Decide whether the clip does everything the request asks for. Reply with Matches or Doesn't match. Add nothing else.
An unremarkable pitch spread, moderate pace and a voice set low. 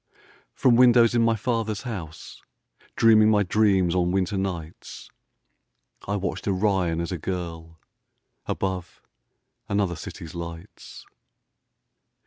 Doesn't match